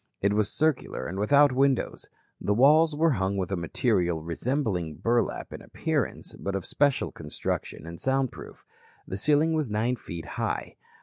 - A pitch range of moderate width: No, wide, 6.9 semitones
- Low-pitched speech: Yes, low, 115 Hz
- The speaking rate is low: No, average, 165 wpm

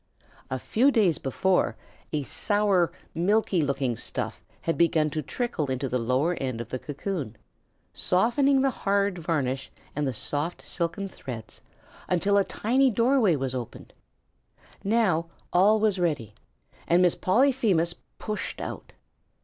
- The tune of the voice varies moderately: No, wide, 6.8 semitones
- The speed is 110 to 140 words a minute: Yes, slow, 135 wpm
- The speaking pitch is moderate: Yes, medium, 175 Hz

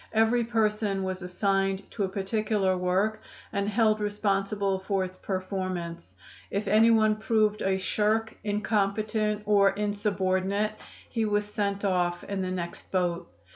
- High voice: Yes, high, 200 Hz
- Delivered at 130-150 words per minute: Yes, slow, 135 wpm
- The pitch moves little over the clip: Yes, narrow, 2.0 semitones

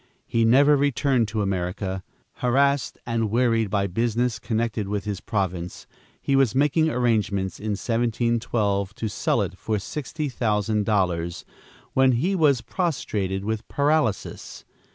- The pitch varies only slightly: No, average, 4.4 semitones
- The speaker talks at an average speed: No, slow, 130 wpm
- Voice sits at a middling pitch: No, low, 115 Hz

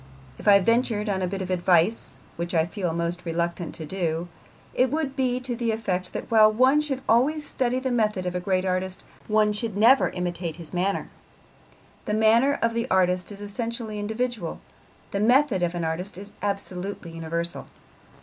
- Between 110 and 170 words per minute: No, average, 180 wpm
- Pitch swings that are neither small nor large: Yes, average, 4.6 semitones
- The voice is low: No, high, 200 Hz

